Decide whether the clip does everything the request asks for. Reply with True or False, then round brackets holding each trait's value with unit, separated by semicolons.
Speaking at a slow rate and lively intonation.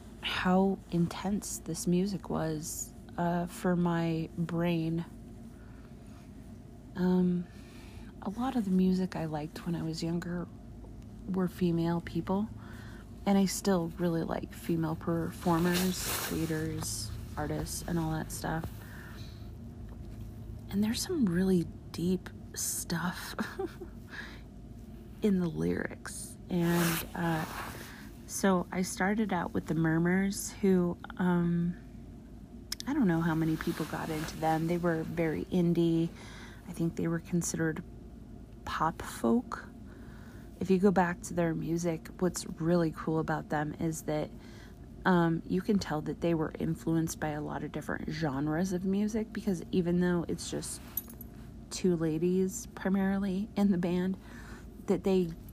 True (130 wpm; 7.3 semitones)